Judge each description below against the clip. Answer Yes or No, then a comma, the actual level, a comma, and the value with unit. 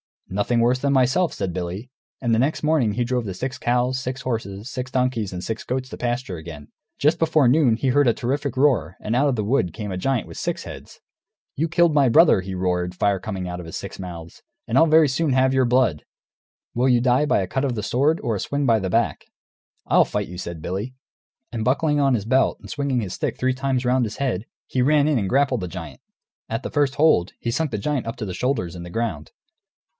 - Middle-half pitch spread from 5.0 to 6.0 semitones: Yes, wide, 5.6 semitones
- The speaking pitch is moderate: No, low, 125 Hz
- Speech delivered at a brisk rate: Yes, fast, 240 wpm